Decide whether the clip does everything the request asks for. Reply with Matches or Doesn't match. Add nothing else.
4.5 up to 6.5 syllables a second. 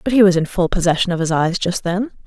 Matches